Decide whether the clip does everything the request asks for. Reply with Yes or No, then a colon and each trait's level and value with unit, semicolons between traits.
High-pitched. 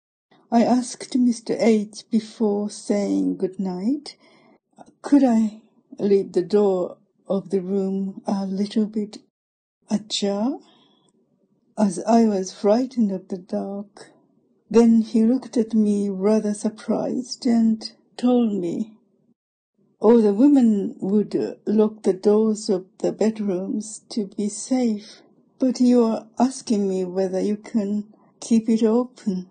Yes: high, 215 Hz